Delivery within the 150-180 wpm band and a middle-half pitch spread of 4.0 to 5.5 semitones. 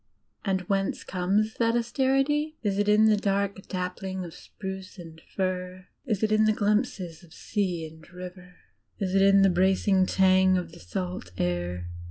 No: average, 170 wpm; narrow, 2.4 semitones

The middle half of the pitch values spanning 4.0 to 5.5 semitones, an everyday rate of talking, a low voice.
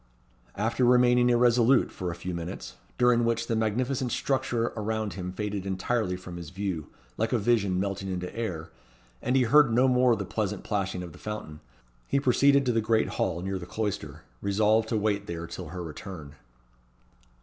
Yes: average, 4.6 semitones; average, 180 wpm; low, 105 Hz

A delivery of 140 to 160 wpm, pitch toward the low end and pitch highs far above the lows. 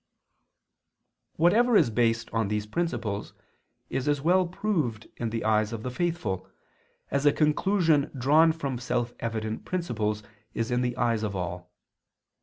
Yes: average, 145 wpm; low, 120 Hz; wide, 6.6 semitones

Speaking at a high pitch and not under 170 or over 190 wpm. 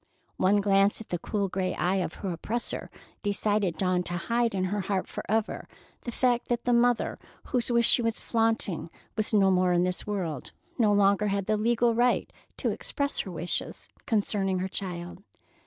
Yes: high, 200 Hz; average, 180 wpm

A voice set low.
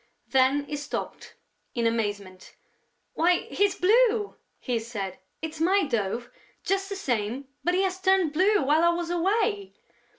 No: very high, 325 Hz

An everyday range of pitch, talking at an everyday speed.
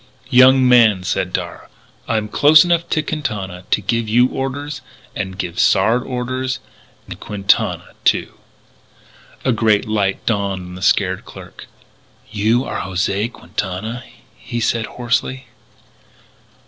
No: average, 4.6 semitones; slow, 125 wpm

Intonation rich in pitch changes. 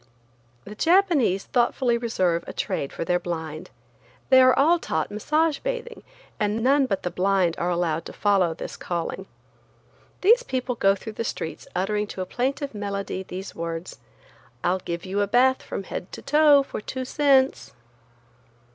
Yes: wide, 6.7 semitones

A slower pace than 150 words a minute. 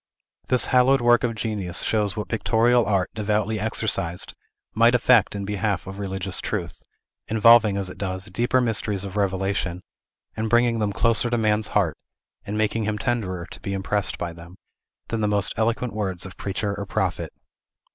No: average, 170 wpm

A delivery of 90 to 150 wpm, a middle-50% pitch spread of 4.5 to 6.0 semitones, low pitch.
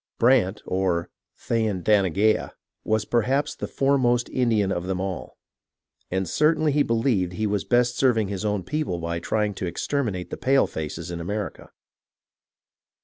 Yes: average, 140 wpm; average, 4.8 semitones; low, 105 Hz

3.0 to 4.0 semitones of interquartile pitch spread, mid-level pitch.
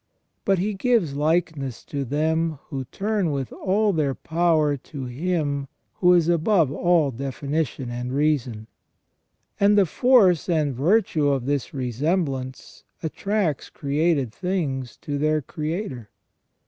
No: average, 4.5 semitones; medium, 155 Hz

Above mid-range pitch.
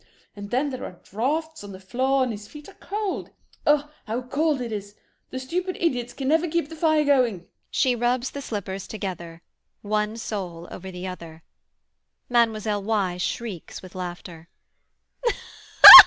Yes: high, 225 Hz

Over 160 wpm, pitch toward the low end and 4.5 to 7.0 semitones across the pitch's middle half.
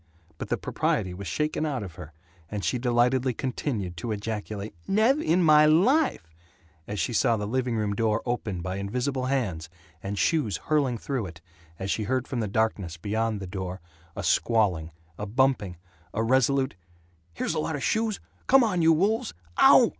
Yes: average, 175 wpm; low, 115 Hz; wide, 5.6 semitones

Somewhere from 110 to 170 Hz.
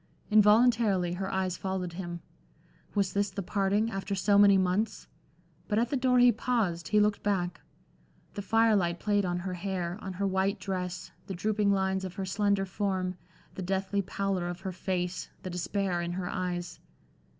No: high, 190 Hz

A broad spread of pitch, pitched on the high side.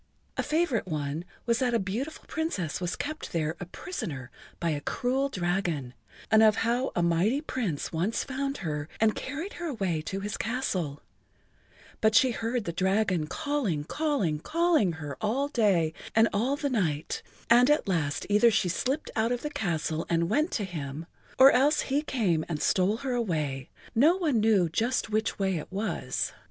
Yes: wide, 7.7 semitones; high, 215 Hz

